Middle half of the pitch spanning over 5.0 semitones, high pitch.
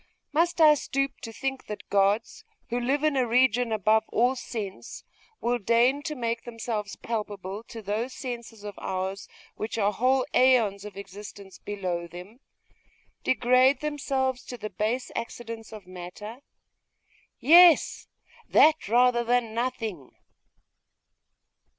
No: average, 3.7 semitones; high, 230 Hz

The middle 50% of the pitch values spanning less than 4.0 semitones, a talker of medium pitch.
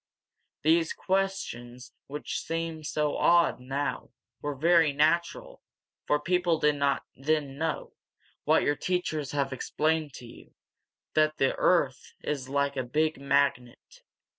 Yes: average, 2.8 semitones; medium, 150 Hz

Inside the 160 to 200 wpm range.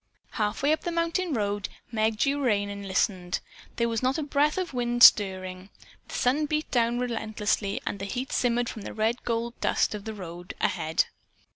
Yes: average, 185 wpm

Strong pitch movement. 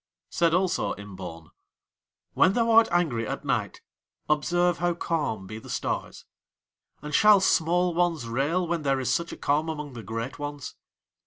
Yes: wide, 6.1 semitones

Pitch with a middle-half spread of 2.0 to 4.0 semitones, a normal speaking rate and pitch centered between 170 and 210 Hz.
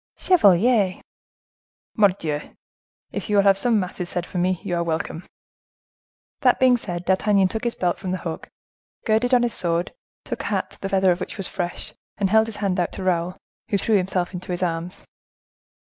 Yes: average, 2.9 semitones; average, 190 wpm; medium, 185 Hz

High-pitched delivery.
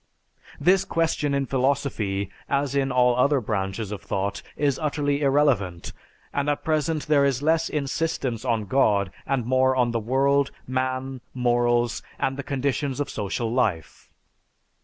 No: low, 130 Hz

